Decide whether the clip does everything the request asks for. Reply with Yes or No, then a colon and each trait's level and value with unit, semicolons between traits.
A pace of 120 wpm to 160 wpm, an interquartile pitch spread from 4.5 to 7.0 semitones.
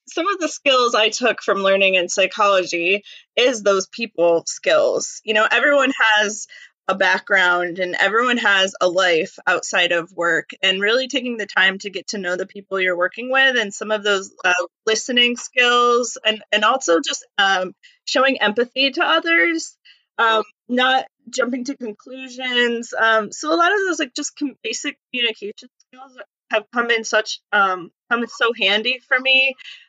No: average, 170 wpm; average, 4.8 semitones